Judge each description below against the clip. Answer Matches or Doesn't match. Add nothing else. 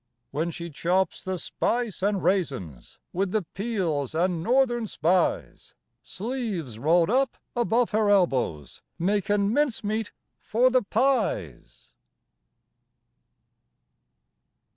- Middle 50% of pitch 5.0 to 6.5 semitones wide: Matches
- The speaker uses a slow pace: Matches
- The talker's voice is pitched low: Doesn't match